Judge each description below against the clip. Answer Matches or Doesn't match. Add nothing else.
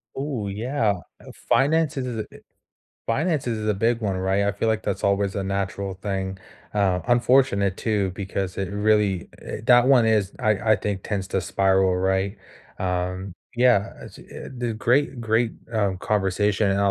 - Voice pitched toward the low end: Matches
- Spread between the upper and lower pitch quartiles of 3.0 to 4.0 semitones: Matches